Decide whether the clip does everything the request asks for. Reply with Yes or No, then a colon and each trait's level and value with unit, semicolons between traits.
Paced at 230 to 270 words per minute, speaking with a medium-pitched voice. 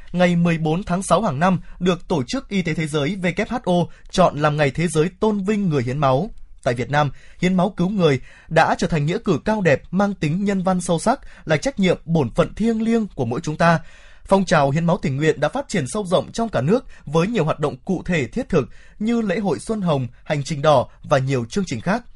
Yes: average, 245 wpm; medium, 175 Hz